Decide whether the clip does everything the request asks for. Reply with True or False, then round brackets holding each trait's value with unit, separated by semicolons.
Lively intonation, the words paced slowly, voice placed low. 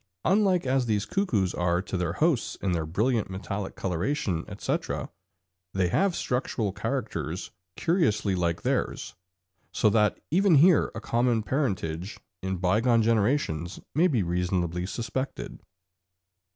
True (6.8 semitones; 125 wpm; 105 Hz)